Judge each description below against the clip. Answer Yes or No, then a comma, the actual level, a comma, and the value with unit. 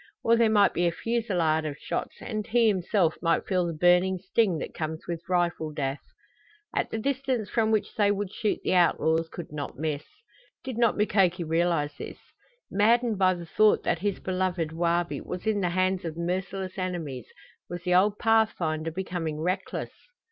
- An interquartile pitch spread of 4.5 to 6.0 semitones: No, average, 3.9 semitones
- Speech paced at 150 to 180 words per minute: Yes, average, 175 wpm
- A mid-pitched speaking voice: Yes, medium, 180 Hz